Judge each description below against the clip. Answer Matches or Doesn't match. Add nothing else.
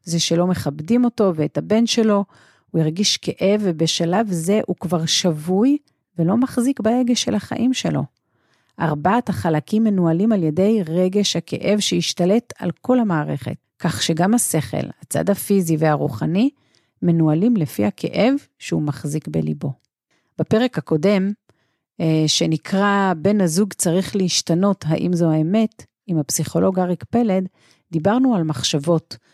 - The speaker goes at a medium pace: Matches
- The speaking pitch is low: Doesn't match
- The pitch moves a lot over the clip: Doesn't match